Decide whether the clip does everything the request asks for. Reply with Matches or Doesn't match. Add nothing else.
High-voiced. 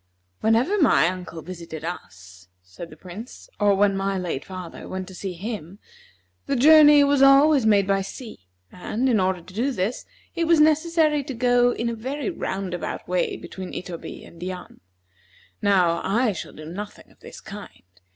Matches